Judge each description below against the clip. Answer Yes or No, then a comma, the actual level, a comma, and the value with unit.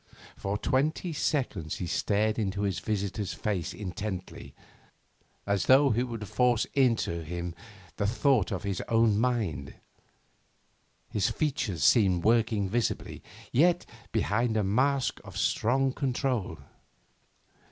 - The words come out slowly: Yes, slow, 120 wpm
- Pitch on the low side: Yes, low, 110 Hz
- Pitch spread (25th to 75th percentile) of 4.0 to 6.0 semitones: Yes, average, 4.5 semitones